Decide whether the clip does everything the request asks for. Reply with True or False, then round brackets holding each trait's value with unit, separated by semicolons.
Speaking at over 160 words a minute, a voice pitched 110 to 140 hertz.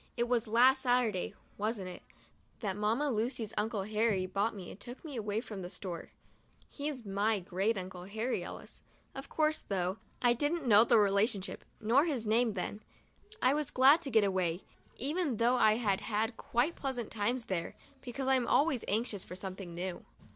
False (180 wpm; 220 Hz)